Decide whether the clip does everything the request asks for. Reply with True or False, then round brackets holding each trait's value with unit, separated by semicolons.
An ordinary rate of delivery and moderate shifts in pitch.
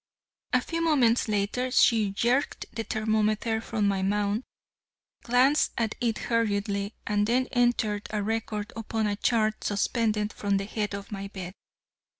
False (150 wpm; 2.3 semitones)